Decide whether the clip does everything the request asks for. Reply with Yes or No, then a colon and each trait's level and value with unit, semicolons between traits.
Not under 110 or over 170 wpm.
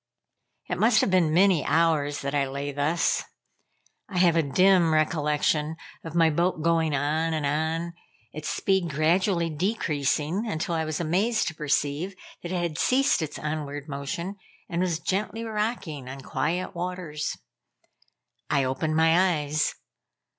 Yes: average, 145 wpm